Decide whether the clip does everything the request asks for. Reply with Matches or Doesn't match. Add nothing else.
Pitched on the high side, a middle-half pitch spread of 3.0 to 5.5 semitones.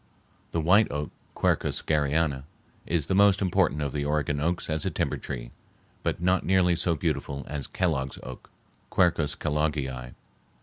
Doesn't match